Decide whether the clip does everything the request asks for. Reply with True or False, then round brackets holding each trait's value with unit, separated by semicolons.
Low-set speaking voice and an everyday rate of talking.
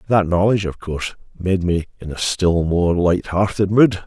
True (90 Hz; 175 wpm)